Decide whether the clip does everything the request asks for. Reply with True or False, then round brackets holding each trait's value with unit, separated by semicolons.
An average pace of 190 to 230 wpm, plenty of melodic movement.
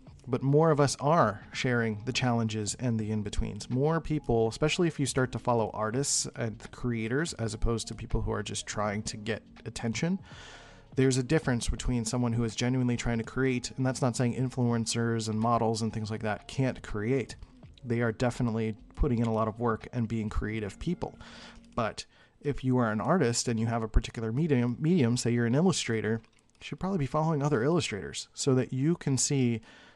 False (200 wpm; 2.9 semitones)